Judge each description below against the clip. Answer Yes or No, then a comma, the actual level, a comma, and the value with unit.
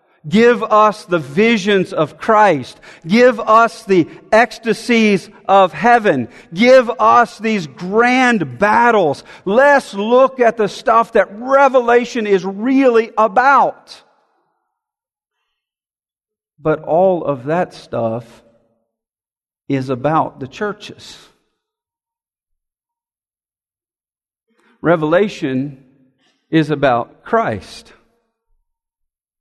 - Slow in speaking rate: Yes, slow, 80 wpm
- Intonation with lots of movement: Yes, wide, 6.9 semitones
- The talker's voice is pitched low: No, high, 215 Hz